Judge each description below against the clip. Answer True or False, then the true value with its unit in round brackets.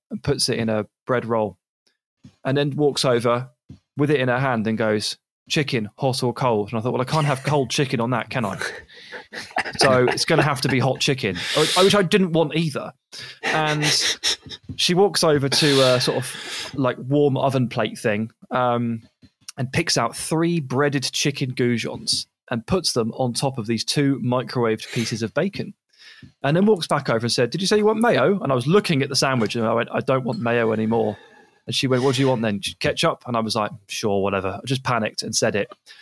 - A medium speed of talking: False (220 wpm)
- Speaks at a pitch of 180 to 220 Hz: False (130 Hz)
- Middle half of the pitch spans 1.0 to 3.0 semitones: False (4.3 semitones)